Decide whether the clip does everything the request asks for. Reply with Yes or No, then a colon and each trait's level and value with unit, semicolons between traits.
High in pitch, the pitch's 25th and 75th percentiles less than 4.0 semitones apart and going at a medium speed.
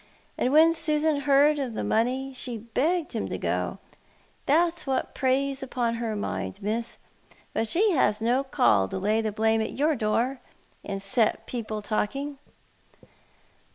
No: very high, 250 Hz; average, 4.5 semitones; average, 155 wpm